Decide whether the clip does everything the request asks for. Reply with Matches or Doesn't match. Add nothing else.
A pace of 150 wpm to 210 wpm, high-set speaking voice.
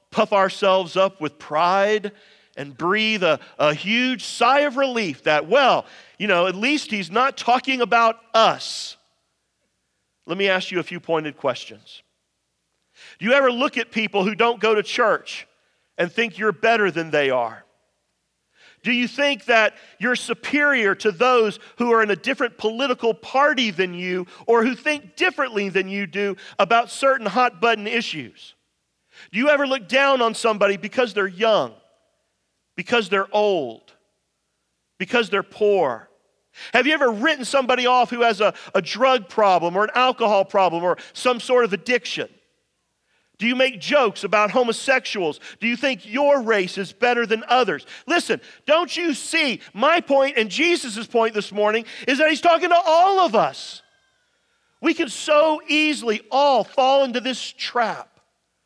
Matches